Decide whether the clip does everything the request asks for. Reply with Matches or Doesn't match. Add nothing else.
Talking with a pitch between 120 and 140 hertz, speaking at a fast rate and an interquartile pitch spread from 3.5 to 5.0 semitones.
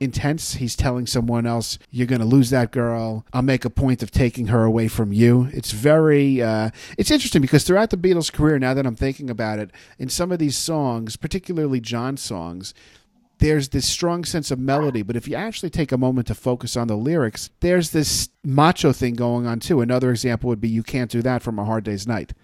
Matches